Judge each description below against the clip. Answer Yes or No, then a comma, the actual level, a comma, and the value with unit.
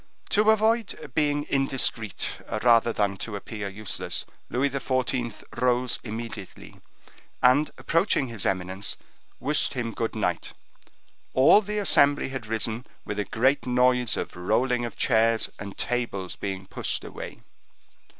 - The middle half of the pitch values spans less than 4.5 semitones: Yes, average, 3.9 semitones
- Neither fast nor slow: No, slow, 130 wpm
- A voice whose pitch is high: No, low, 120 Hz